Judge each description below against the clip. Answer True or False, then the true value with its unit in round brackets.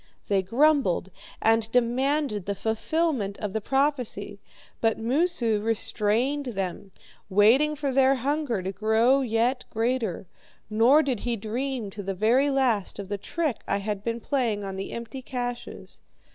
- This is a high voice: True (230 Hz)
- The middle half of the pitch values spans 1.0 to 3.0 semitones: False (4.6 semitones)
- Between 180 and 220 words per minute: False (145 wpm)